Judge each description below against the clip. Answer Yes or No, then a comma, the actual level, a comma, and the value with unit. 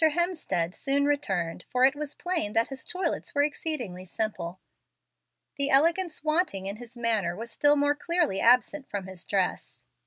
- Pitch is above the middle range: Yes, very high, 270 Hz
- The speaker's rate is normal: Yes, average, 160 wpm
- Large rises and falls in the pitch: Yes, wide, 7.0 semitones